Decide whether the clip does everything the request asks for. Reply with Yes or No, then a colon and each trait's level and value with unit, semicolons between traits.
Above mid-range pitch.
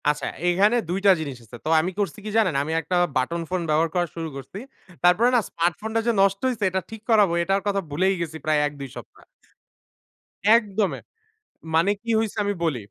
No: medium, 180 Hz